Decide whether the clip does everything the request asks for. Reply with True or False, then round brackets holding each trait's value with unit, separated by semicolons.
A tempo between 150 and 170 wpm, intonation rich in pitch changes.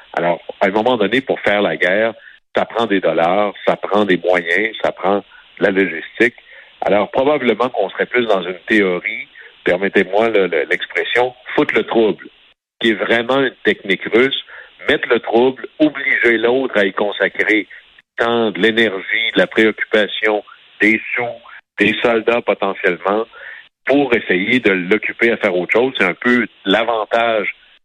False (160 wpm; 2.7 semitones)